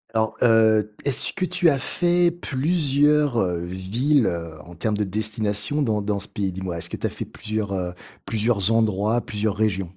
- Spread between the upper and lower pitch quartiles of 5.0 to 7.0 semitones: Yes, wide, 5.6 semitones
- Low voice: Yes, low, 110 Hz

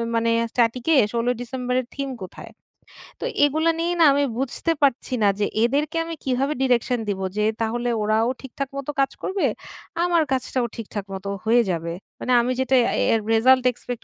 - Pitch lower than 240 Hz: No, very high, 250 Hz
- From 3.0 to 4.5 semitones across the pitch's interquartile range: Yes, average, 3.3 semitones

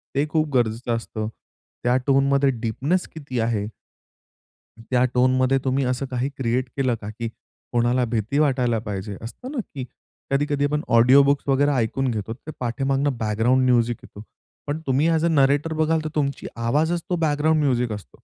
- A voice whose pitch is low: Yes, low, 130 Hz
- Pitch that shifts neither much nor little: Yes, average, 3.5 semitones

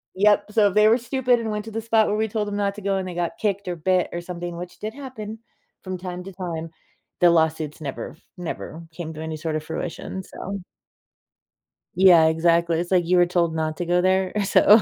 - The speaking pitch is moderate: Yes, medium, 180 Hz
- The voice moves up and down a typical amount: Yes, average, 3.5 semitones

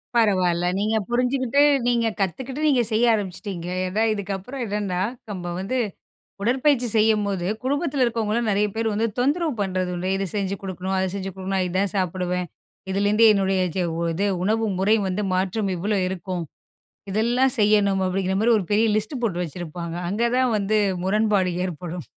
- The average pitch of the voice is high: Yes, high, 200 Hz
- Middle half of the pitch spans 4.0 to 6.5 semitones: No, average, 3.4 semitones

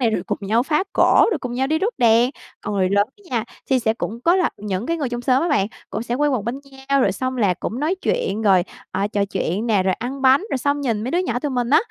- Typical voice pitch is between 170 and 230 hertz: No, high, 245 Hz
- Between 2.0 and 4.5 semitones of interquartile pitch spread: No, average, 4.9 semitones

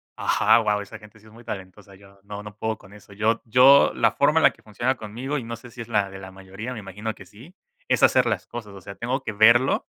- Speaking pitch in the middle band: No, low, 110 Hz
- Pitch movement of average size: Yes, average, 3.0 semitones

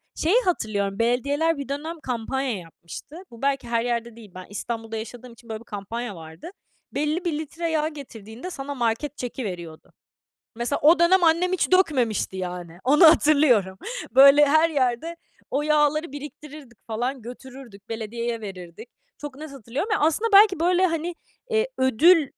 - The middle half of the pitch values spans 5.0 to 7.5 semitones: Yes, wide, 5.5 semitones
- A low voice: No, very high, 265 Hz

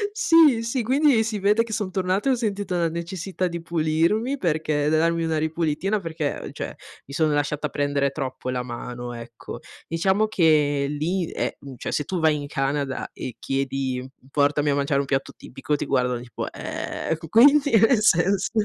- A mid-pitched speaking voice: Yes, medium, 160 Hz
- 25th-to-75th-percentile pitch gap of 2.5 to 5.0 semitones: No, wide, 6.0 semitones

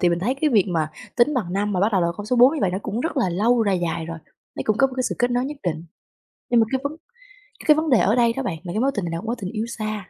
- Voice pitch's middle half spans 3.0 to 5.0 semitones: No, wide, 5.5 semitones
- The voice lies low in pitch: No, high, 215 Hz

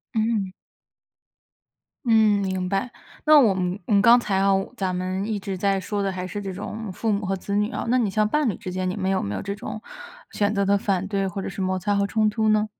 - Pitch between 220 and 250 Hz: No, high, 200 Hz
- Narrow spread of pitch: Yes, narrow, 2.1 semitones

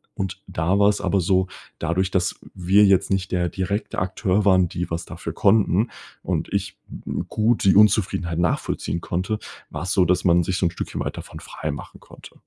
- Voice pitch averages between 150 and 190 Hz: No, very low, 95 Hz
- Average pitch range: No, narrow, 2.3 semitones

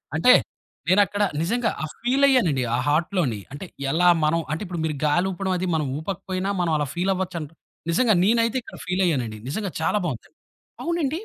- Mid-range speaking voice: Yes, medium, 180 Hz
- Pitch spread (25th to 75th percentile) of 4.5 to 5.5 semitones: Yes, average, 5.0 semitones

